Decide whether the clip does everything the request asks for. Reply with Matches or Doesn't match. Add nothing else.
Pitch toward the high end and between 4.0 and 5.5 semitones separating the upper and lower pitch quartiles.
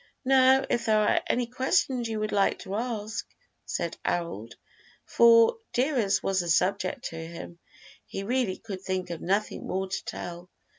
Matches